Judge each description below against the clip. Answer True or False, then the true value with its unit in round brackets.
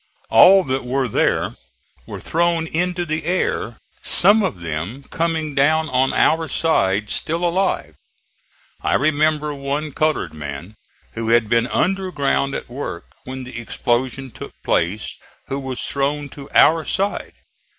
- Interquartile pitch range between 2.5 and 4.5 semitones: False (5.2 semitones)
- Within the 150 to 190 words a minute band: False (140 wpm)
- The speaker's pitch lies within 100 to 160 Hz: True (140 Hz)